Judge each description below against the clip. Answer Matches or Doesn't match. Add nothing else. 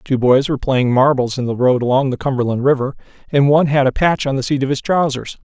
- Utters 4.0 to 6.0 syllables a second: Doesn't match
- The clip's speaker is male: Matches